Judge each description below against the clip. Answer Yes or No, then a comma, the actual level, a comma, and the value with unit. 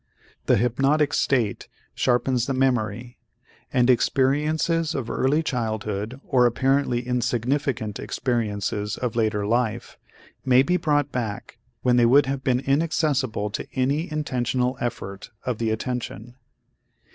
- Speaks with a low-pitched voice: Yes, low, 125 Hz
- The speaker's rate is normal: No, slow, 125 wpm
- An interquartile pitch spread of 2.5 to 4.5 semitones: Yes, average, 2.9 semitones